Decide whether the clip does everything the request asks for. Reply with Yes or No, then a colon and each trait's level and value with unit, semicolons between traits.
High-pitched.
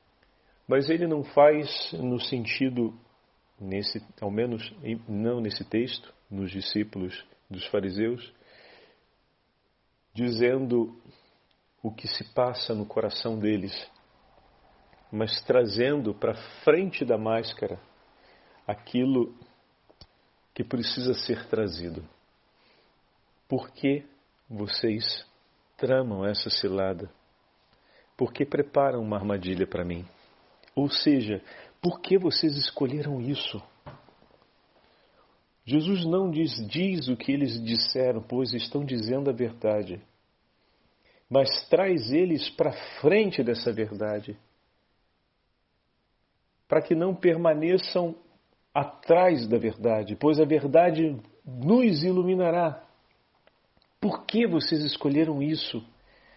No: low, 120 Hz